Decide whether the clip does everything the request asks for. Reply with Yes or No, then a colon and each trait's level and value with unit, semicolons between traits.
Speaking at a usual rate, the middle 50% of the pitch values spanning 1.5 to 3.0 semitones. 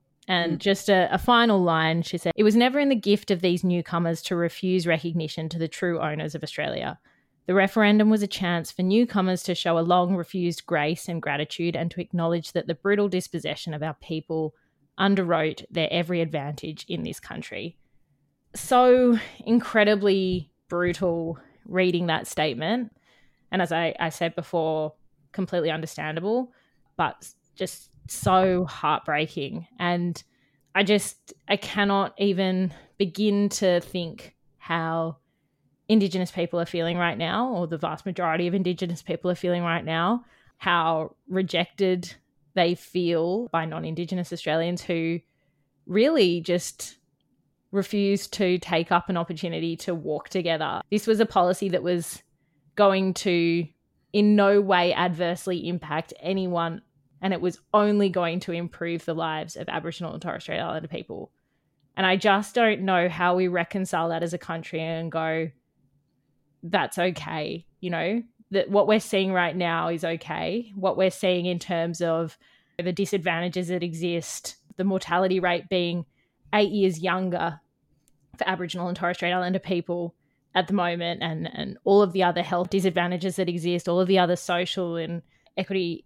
Yes: average, 155 wpm; narrow, 2.5 semitones